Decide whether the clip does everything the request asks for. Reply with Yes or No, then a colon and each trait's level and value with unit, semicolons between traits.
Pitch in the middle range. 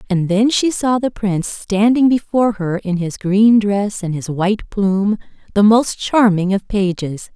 No: high, 205 Hz